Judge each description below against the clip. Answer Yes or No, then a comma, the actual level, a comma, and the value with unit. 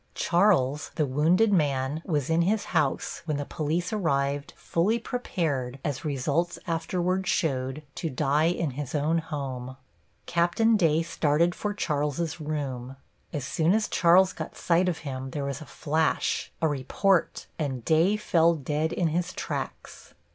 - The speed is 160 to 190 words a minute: No, average, 150 wpm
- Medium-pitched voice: Yes, medium, 155 Hz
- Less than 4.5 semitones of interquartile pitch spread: Yes, average, 3.5 semitones